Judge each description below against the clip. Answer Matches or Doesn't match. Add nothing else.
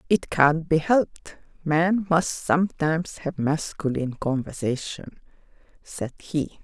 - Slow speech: Matches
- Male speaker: Doesn't match